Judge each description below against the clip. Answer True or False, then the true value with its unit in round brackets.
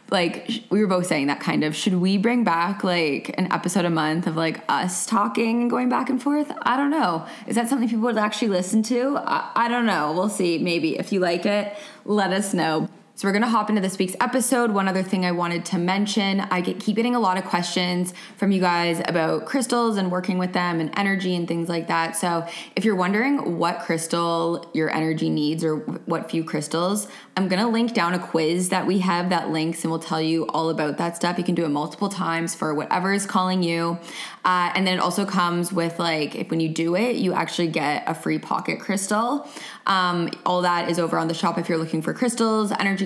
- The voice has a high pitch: False (180 Hz)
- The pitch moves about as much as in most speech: True (3.7 semitones)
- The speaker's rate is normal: False (235 wpm)